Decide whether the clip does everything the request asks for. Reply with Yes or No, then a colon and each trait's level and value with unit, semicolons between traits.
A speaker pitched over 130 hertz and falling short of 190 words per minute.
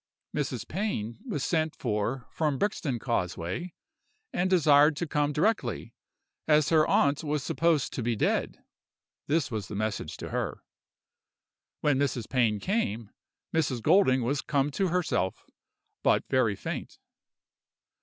Yes: medium, 140 Hz; slow, 135 wpm